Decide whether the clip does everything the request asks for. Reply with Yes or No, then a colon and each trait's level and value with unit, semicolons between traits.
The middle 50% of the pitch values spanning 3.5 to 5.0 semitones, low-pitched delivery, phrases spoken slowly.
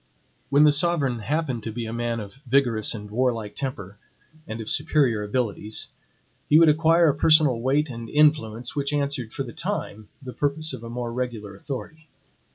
No: average, 4.7 semitones; low, 125 Hz; average, 175 wpm